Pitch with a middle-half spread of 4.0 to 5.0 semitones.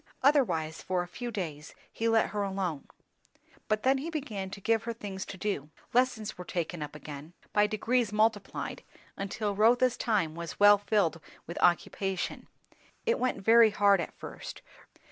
Yes: average, 4.3 semitones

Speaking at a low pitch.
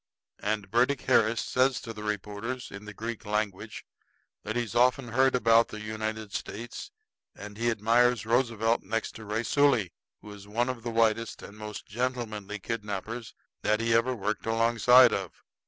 Yes: low, 115 Hz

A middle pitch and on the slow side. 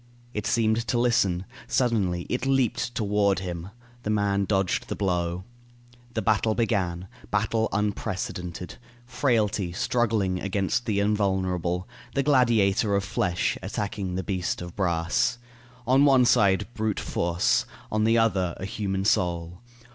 No: low, 100 Hz; slow, 130 wpm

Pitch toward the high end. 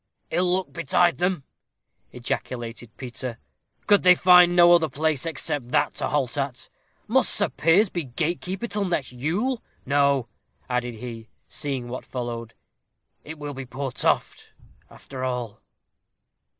No: medium, 140 Hz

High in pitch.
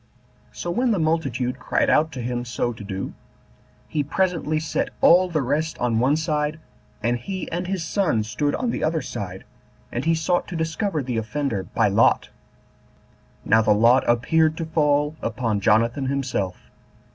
No: medium, 145 Hz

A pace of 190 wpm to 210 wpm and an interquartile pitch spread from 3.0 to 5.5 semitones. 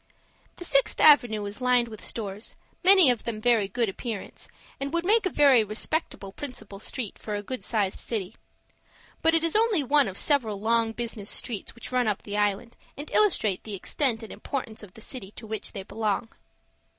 Yes: average, 195 wpm; average, 4.8 semitones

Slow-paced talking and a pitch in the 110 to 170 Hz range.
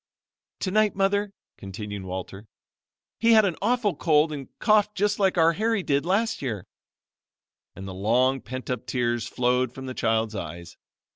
No: average, 155 wpm; low, 135 Hz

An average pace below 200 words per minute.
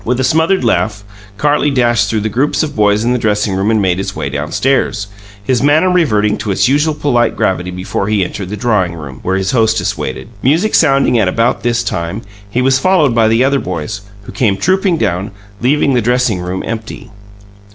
No: fast, 205 wpm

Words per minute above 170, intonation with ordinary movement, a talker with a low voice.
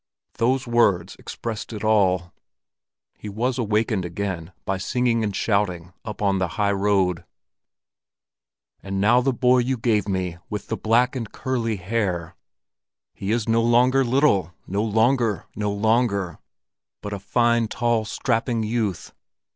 No: average, 140 wpm; average, 3.4 semitones; low, 110 Hz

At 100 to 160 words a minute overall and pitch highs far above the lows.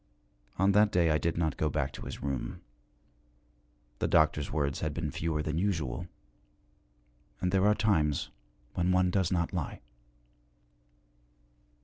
No: average, 140 wpm; average, 3.2 semitones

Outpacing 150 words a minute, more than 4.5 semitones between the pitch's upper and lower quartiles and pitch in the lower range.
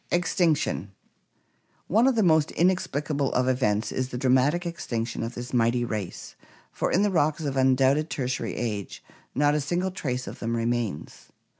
Yes: average, 170 wpm; average, 5.1 semitones; low, 130 Hz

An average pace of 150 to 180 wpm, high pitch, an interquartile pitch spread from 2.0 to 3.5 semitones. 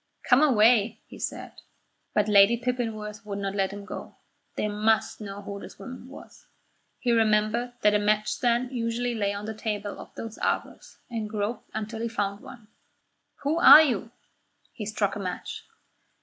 Yes: average, 170 wpm; high, 215 Hz; narrow, 2.4 semitones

